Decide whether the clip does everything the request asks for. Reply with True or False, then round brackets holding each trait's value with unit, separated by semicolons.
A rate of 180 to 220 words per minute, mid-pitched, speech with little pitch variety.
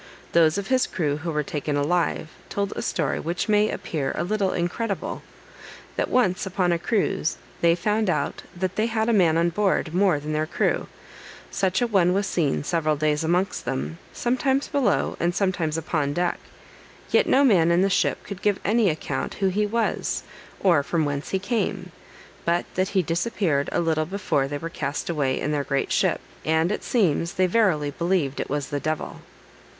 False (190 wpm; 175 Hz; 4.4 semitones)